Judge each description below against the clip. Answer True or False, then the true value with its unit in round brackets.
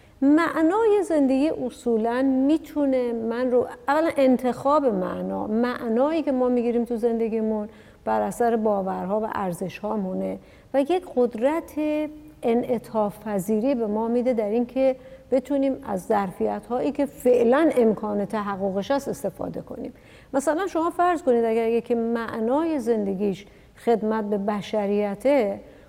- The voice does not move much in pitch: False (4.5 semitones)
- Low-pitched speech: False (240 Hz)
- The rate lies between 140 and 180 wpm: False (115 wpm)